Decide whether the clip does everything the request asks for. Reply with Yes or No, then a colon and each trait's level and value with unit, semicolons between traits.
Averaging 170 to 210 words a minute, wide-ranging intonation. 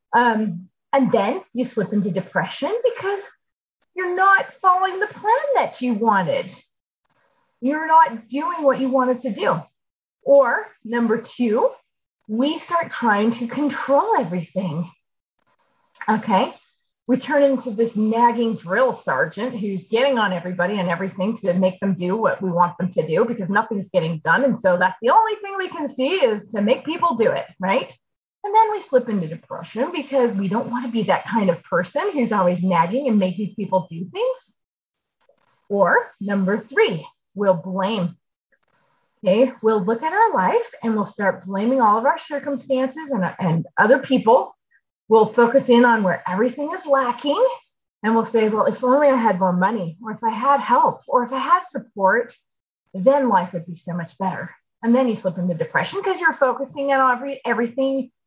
Yes: average, 175 wpm; wide, 7.0 semitones